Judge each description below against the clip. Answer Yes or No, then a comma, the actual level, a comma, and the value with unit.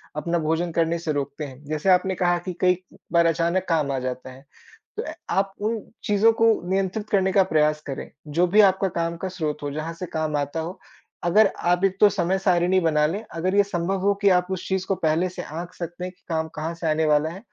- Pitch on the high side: No, medium, 175 Hz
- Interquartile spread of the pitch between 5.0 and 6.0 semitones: No, average, 3.4 semitones